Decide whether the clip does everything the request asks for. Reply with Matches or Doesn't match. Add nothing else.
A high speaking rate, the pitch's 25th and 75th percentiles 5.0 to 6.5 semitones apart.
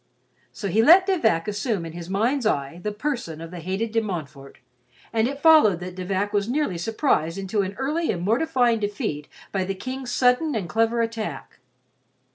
Doesn't match